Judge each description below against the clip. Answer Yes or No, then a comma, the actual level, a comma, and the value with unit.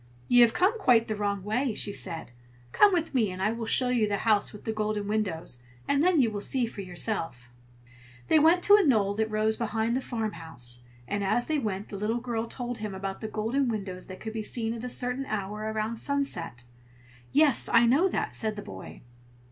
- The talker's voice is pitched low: No, high, 220 Hz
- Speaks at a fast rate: Yes, fast, 215 wpm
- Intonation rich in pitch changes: No, average, 3.5 semitones